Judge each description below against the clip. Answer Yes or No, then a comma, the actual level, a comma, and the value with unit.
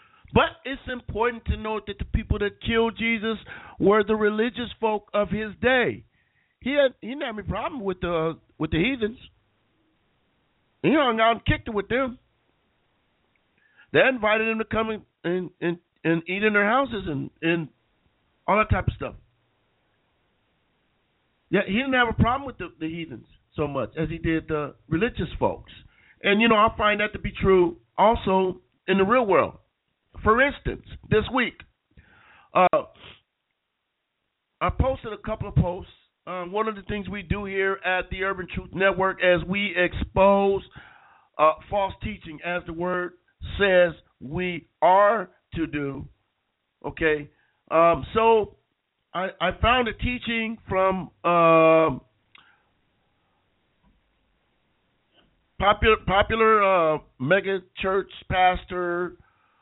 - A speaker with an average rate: Yes, average, 145 wpm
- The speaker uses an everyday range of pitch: Yes, average, 4.7 semitones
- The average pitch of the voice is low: No, high, 195 Hz